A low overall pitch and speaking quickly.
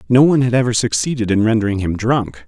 Yes: low, 115 Hz; fast, 220 wpm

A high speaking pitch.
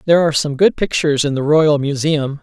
No: medium, 150 Hz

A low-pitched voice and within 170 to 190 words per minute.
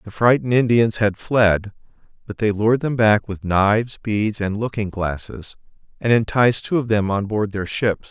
Yes: low, 105 Hz; average, 185 wpm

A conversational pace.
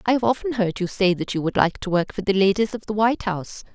No: fast, 305 wpm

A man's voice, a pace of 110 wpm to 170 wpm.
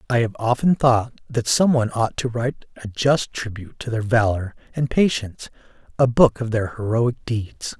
No: male; average, 185 wpm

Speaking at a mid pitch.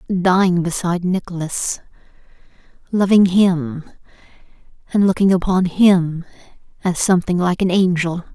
Yes: medium, 180 Hz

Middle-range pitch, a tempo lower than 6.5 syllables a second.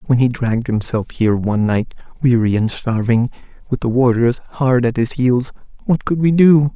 No: low, 125 Hz; 5.1 syllables/s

